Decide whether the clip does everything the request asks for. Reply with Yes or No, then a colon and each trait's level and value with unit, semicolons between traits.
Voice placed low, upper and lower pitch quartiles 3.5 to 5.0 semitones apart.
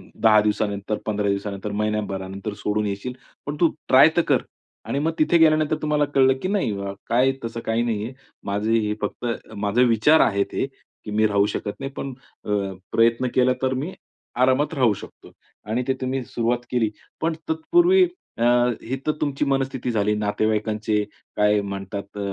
Yes: low, 115 Hz; average, 4.5 semitones